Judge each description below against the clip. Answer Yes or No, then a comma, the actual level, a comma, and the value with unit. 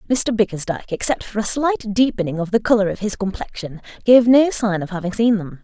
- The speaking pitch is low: No, high, 210 Hz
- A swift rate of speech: Yes, fast, 215 wpm